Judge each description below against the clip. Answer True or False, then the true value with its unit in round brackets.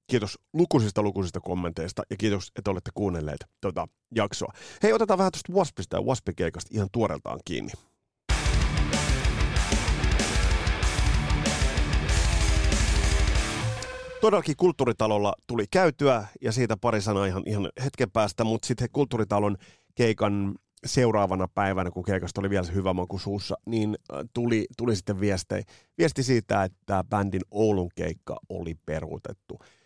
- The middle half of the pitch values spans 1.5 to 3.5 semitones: False (4.0 semitones)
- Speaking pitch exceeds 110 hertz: False (105 Hz)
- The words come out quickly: False (120 wpm)